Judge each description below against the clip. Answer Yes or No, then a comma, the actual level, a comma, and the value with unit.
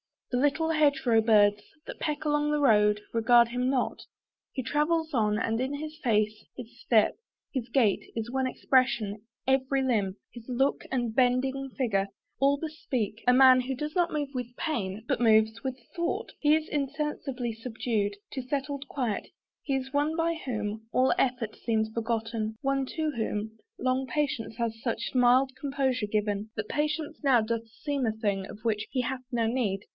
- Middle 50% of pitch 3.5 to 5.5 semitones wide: Yes, average, 3.8 semitones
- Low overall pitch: No, very high, 250 Hz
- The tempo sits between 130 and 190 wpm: Yes, average, 175 wpm